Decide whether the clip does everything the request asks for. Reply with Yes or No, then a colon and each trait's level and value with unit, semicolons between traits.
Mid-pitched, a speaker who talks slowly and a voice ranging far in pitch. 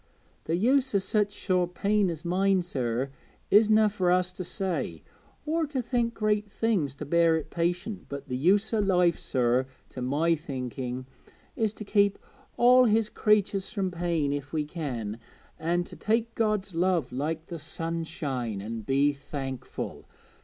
No: medium, 175 Hz; average, 160 wpm; wide, 6.6 semitones